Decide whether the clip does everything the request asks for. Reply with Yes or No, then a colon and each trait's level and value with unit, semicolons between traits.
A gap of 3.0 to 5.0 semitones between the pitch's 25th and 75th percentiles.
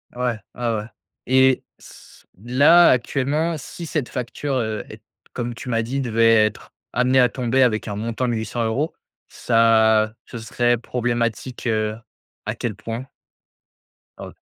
No: narrow, 2.5 semitones